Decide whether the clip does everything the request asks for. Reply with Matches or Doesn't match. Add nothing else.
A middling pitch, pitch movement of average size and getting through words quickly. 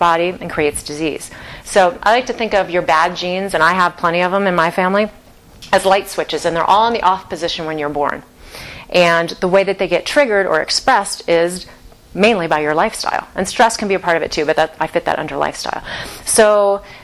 Matches